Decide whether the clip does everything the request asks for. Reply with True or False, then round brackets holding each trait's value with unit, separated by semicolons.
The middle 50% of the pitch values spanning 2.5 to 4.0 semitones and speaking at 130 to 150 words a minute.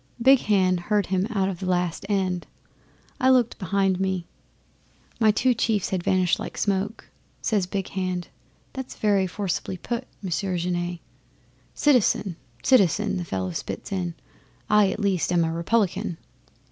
False (2.8 semitones; 160 wpm)